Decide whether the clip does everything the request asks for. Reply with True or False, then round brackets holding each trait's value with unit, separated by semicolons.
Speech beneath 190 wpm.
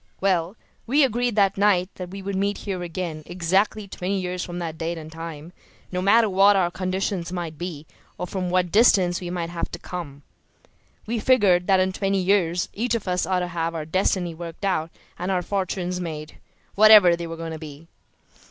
False (200 wpm)